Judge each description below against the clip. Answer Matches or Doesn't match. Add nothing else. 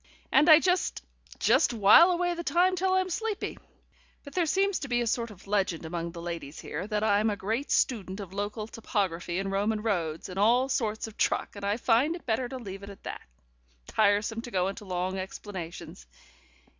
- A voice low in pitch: Doesn't match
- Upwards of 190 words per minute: Matches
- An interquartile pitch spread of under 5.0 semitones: Doesn't match